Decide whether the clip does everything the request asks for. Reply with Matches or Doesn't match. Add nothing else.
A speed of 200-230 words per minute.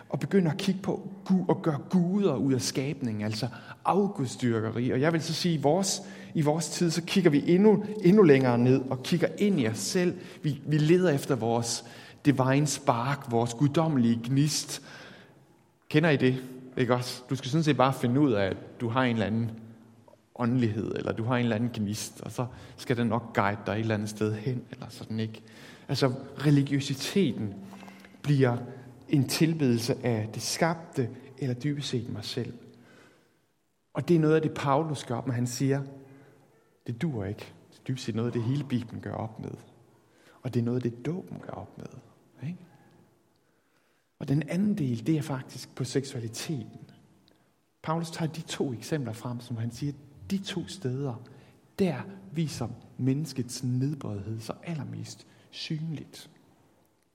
Doesn't match